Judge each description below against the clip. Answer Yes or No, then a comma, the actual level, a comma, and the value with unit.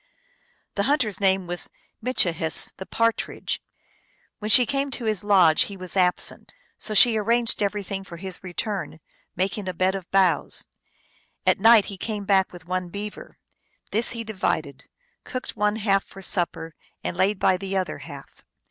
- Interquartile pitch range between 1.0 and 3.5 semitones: Yes, average, 2.7 semitones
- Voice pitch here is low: No, high, 195 Hz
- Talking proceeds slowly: No, average, 165 wpm